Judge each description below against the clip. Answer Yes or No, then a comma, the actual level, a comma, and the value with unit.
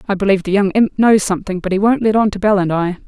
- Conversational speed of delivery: No, fast, 310 wpm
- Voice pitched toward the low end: No, high, 200 Hz